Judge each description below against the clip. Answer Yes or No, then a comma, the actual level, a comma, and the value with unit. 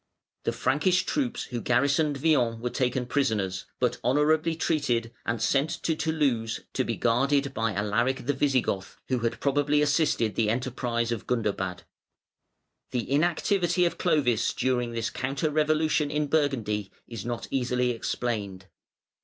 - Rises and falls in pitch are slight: No, average, 4.3 semitones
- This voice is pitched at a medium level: No, low, 130 Hz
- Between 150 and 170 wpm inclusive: No, average, 140 wpm